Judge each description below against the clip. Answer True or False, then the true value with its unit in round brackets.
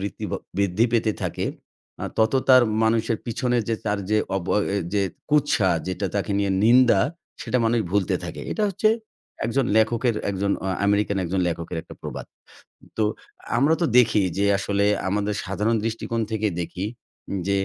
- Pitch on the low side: True (105 Hz)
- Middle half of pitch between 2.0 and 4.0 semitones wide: True (2.8 semitones)